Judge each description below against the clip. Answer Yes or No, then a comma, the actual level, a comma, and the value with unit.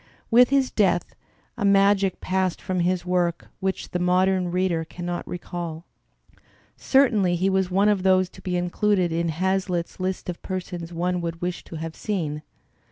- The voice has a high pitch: No, medium, 180 Hz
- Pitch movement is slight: Yes, narrow, 1.7 semitones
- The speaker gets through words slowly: No, average, 165 wpm